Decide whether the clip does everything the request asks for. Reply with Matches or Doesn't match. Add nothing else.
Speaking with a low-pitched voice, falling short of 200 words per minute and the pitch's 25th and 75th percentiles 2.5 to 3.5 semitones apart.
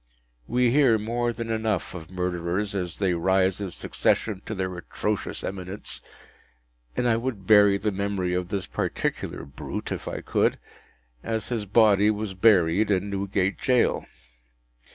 Matches